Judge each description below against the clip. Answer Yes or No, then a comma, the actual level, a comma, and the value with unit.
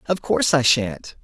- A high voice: No, low, 135 Hz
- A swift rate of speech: No, average, 195 wpm